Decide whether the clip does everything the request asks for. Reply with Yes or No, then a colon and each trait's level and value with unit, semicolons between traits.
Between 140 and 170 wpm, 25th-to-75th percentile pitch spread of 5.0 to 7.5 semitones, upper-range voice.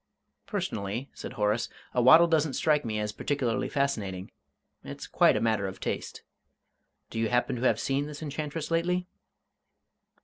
No: average, 150 wpm; wide, 5.6 semitones; low, 130 Hz